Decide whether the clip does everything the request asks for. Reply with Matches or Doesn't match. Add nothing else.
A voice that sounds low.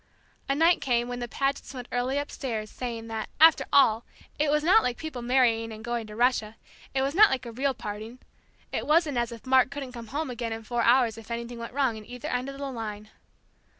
Doesn't match